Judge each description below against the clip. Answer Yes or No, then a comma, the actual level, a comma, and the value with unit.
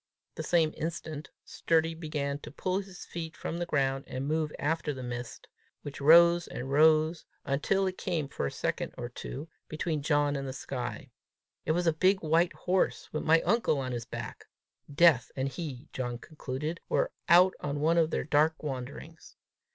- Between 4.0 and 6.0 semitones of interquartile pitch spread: No, average, 3.3 semitones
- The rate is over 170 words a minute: Yes, average, 180 wpm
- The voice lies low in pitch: No, medium, 155 Hz